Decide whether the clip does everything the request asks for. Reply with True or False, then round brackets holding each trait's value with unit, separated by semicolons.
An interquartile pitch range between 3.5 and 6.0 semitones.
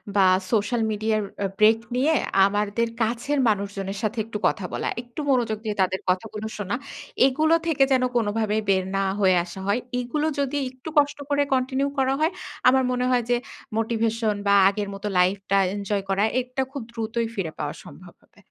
True (3.9 semitones)